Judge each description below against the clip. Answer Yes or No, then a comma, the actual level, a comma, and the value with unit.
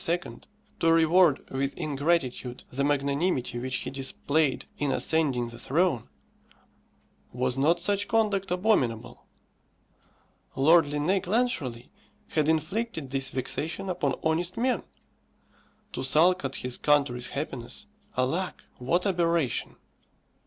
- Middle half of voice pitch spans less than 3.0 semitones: No, average, 4.9 semitones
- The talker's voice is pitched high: No, medium, 150 Hz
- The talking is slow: Yes, slow, 110 wpm